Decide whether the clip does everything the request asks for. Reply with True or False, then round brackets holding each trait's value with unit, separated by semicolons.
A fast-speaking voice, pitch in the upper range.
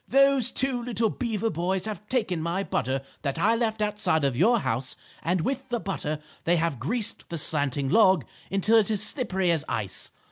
False (185 wpm; 195 Hz)